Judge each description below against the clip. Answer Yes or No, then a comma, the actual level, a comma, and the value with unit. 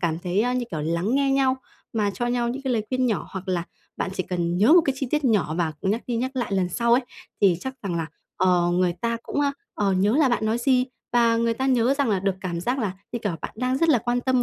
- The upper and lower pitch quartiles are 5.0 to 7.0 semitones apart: Yes, wide, 5.4 semitones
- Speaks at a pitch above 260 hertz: No, high, 230 Hz